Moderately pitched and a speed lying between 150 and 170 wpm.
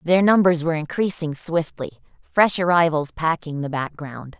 No: medium, 160 Hz; slow, 135 wpm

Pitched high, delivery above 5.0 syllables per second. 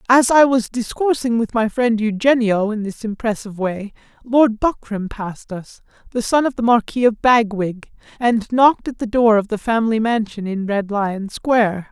No: high, 225 Hz; 4.8 syllables/s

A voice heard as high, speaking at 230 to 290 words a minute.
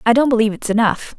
Yes: high, 230 Hz; fast, 255 wpm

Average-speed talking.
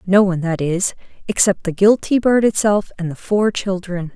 Yes: average, 190 wpm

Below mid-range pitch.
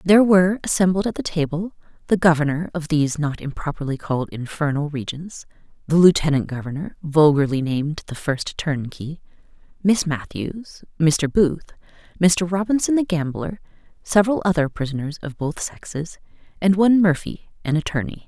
No: medium, 165 Hz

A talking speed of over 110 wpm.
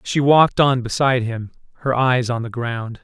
Yes: average, 200 wpm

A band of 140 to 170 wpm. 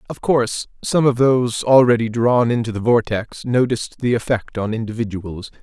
Yes: average, 160 wpm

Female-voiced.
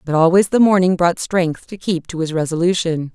Yes: female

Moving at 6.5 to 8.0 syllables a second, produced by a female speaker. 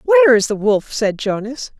Yes: 6.6 syllables/s; female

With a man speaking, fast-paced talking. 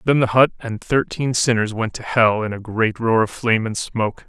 Yes: male; fast, 240 wpm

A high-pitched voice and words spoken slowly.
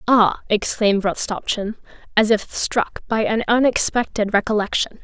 Yes: high, 215 Hz; slow, 120 wpm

